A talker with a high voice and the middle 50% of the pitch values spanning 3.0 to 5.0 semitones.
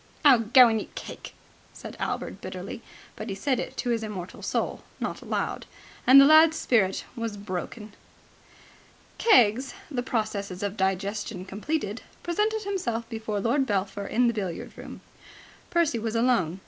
Yes: high, 225 Hz; average, 4.5 semitones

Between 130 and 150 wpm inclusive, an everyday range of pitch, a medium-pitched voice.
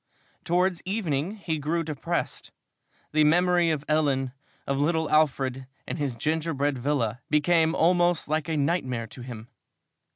Yes: slow, 135 wpm; average, 3.5 semitones; medium, 155 Hz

